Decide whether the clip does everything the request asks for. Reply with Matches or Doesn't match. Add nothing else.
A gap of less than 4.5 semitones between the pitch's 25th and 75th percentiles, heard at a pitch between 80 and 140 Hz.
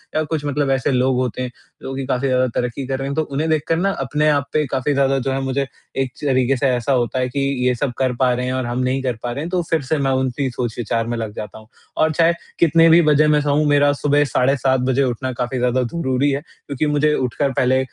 Matches